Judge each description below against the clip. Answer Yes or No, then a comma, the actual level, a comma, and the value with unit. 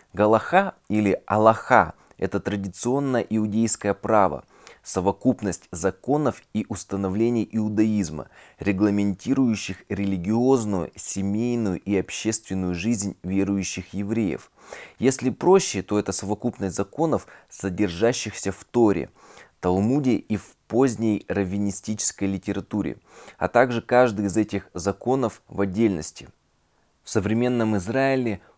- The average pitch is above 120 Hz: No, low, 105 Hz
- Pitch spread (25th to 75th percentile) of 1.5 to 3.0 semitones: Yes, average, 2.7 semitones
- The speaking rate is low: Yes, slow, 95 wpm